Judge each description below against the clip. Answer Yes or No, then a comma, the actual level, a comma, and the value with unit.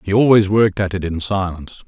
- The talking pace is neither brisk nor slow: No, fast, 225 wpm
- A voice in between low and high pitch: No, very low, 95 Hz